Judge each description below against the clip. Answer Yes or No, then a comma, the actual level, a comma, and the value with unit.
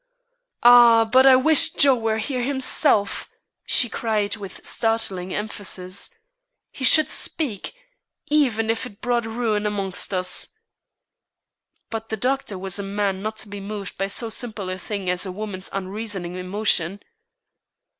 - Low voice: No, high, 215 Hz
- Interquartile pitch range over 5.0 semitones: No, average, 3.6 semitones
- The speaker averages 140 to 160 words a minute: Yes, average, 145 wpm